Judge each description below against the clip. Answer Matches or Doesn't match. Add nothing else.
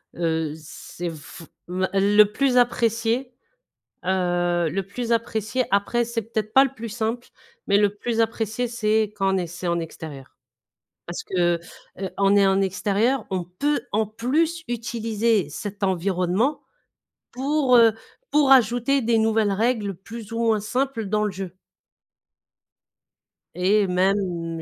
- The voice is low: Doesn't match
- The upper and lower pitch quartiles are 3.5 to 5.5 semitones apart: Matches